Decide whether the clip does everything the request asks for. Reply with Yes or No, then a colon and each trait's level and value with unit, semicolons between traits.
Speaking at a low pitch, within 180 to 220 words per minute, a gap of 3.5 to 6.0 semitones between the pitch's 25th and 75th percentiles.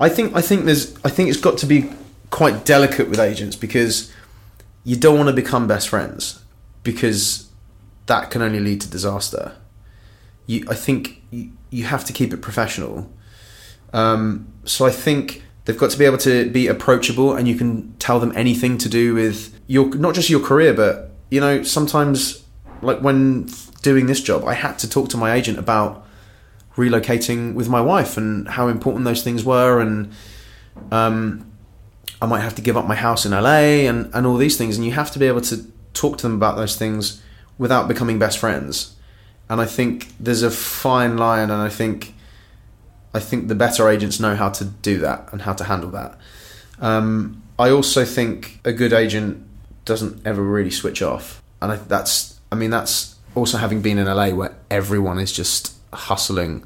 No: low, 110 Hz; average, 190 wpm; average, 2.8 semitones